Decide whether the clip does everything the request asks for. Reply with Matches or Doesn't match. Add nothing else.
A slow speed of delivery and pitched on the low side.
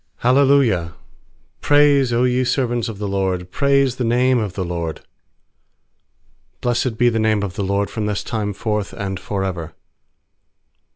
Doesn't match